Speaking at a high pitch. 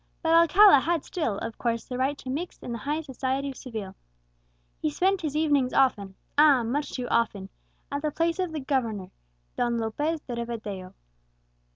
Yes: very high, 265 Hz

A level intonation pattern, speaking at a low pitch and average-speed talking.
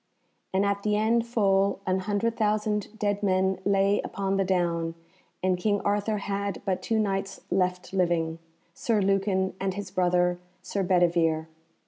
No: narrow, 1.9 semitones; high, 195 Hz; average, 150 wpm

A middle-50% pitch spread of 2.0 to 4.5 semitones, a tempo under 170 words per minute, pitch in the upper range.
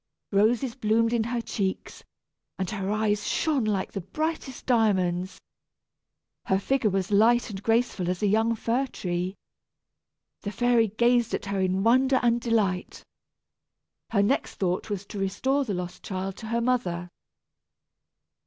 Yes: average, 3.7 semitones; average, 145 wpm; high, 215 Hz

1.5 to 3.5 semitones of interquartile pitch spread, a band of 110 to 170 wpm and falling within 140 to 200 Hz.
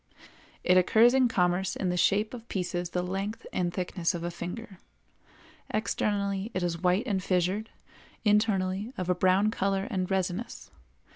Yes: average, 2.7 semitones; average, 155 wpm; high, 190 Hz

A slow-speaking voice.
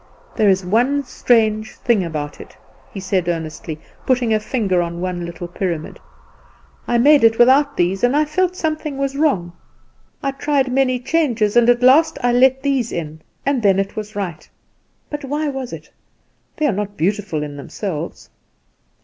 No: average, 170 wpm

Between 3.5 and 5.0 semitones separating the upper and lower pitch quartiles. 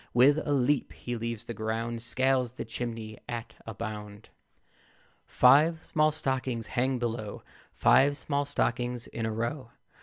No: average, 2.7 semitones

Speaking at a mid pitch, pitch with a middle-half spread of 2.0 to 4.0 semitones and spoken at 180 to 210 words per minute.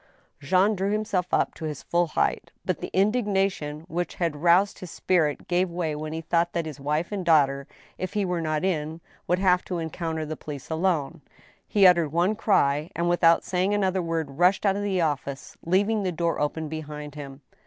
Yes: medium, 170 Hz; average, 3.4 semitones; average, 195 wpm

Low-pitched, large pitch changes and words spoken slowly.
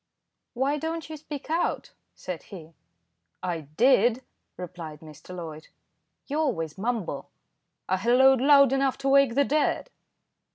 No: high, 245 Hz; wide, 7.8 semitones; slow, 130 wpm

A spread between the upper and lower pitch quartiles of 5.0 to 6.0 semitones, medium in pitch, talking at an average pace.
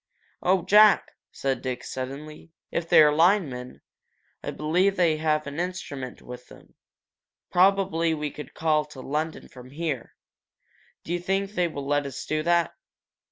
No: average, 3.9 semitones; medium, 155 Hz; average, 150 wpm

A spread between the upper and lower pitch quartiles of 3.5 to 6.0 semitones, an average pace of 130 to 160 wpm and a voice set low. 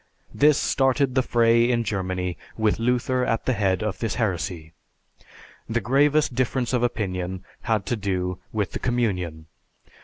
Yes: average, 4.9 semitones; average, 150 wpm; low, 115 Hz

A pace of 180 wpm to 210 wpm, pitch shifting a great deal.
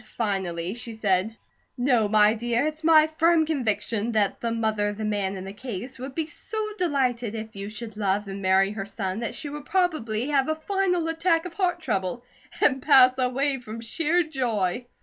Yes: average, 190 wpm; wide, 6.4 semitones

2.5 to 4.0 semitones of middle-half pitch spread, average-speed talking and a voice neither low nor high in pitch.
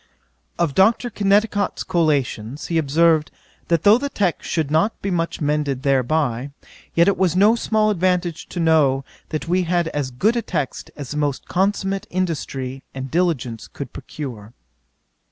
No: average, 5.2 semitones; average, 155 wpm; medium, 165 Hz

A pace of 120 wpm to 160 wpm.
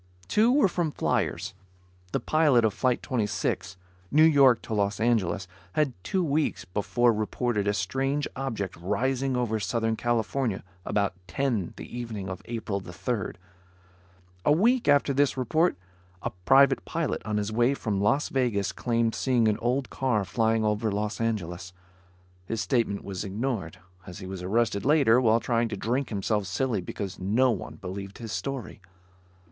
Yes: average, 155 wpm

